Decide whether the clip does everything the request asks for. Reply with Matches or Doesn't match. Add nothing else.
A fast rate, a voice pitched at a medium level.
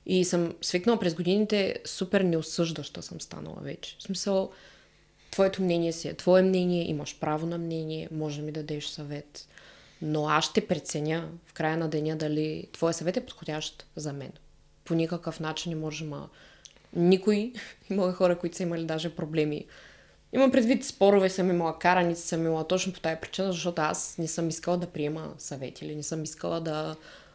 Matches